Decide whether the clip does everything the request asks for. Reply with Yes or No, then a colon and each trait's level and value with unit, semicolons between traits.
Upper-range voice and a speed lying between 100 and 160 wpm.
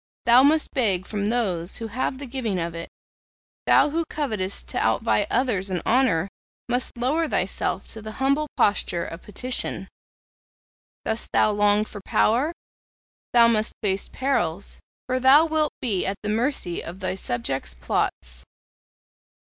Yes: high, 220 Hz; average, 145 wpm